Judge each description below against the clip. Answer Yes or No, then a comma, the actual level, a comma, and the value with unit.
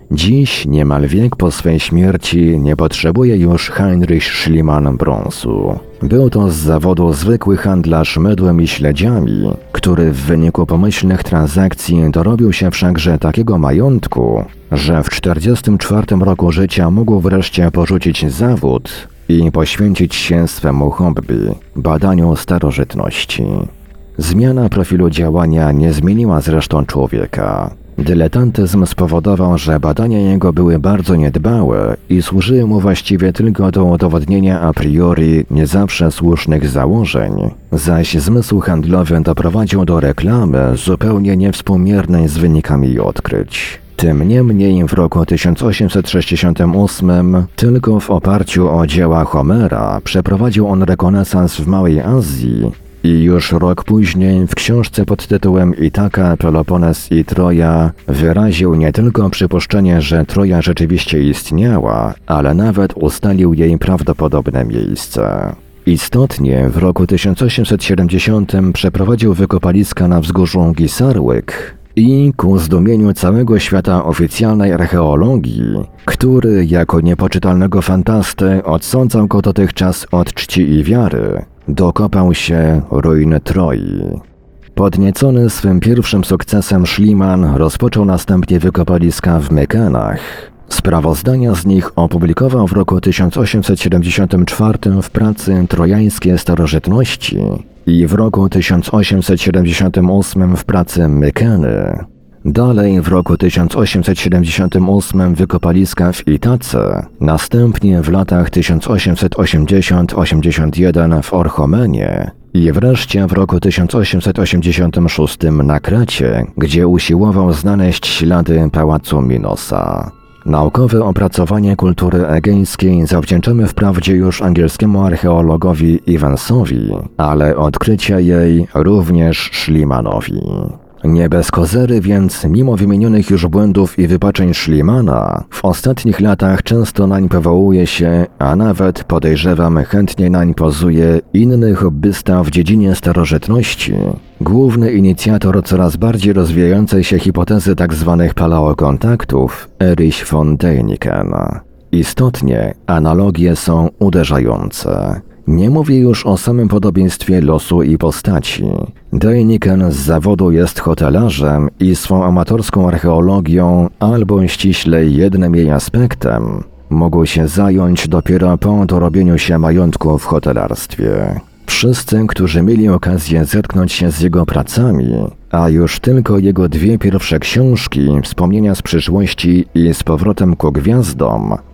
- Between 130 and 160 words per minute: No, slow, 110 wpm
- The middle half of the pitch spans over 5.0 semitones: No, average, 3.3 semitones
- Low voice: Yes, very low, 90 Hz